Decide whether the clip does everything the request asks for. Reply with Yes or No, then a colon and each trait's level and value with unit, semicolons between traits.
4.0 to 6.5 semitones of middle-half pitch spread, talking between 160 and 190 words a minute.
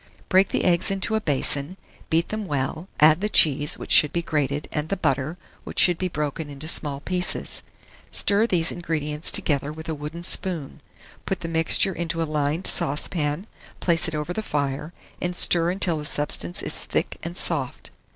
No: average, 3.2 semitones; average, 180 wpm